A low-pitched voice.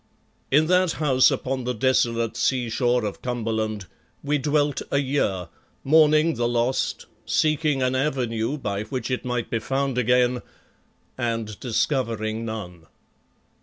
Yes: low, 125 Hz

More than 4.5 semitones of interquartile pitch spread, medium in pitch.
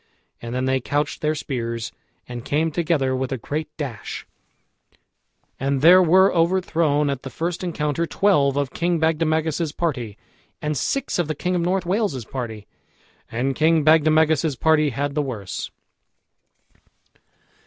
No: average, 3.8 semitones; medium, 150 Hz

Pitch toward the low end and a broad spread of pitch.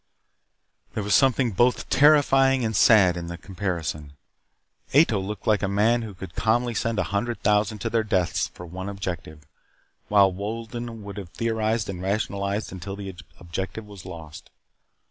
No: low, 100 Hz; average, 3.3 semitones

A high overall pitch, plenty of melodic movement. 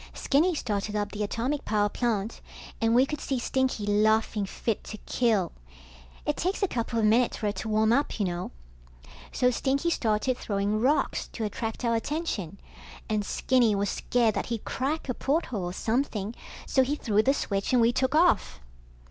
No: high, 225 Hz; average, 3.9 semitones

